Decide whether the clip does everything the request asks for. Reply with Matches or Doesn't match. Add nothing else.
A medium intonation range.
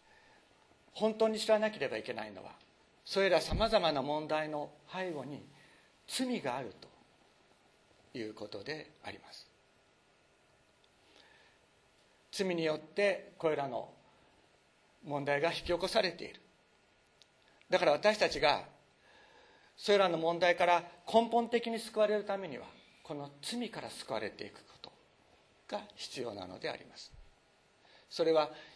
Doesn't match